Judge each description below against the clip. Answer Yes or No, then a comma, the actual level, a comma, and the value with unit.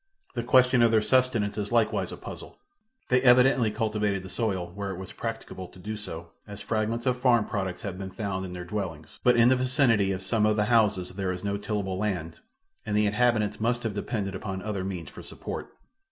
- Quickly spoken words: Yes, fast, 210 wpm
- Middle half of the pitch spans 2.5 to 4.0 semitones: Yes, average, 3.5 semitones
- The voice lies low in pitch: Yes, low, 105 Hz